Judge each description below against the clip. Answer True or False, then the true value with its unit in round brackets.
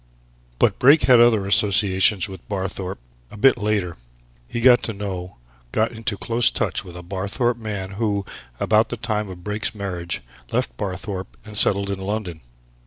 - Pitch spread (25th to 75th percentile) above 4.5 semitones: False (2.7 semitones)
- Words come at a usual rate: True (165 wpm)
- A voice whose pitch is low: True (100 Hz)